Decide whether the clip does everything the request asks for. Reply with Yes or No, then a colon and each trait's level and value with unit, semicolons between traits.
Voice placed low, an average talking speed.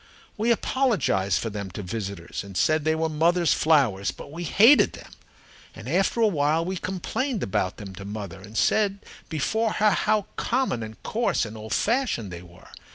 No: medium, 155 Hz; average, 180 wpm